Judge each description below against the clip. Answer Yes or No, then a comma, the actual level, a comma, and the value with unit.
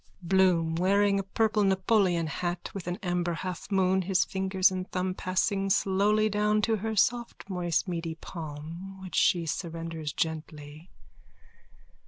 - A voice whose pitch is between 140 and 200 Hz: Yes, medium, 185 Hz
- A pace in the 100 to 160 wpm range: Yes, slow, 135 wpm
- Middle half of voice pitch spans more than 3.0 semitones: No, average, 2.7 semitones